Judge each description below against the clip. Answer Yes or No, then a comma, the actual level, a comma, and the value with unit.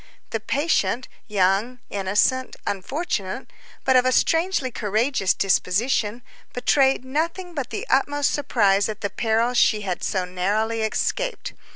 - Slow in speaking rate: Yes, slow, 130 wpm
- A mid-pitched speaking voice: No, high, 230 Hz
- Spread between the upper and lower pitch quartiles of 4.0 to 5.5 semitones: Yes, average, 5.0 semitones